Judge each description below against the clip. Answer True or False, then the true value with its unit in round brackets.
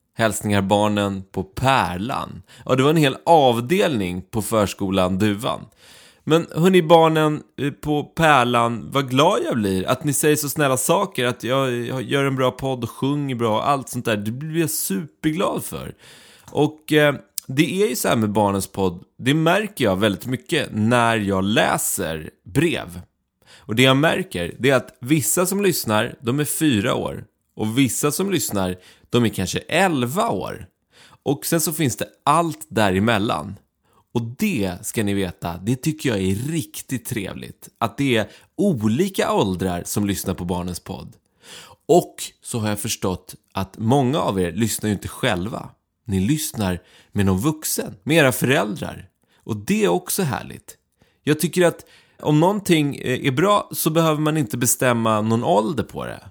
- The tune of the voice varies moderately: False (6.8 semitones)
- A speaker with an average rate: True (170 wpm)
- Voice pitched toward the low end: True (125 Hz)